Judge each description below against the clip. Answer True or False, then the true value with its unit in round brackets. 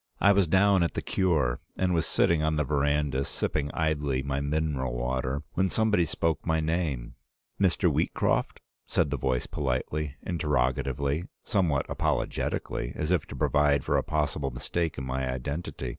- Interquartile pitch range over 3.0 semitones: True (3.6 semitones)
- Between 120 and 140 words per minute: False (160 wpm)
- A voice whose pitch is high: False (75 Hz)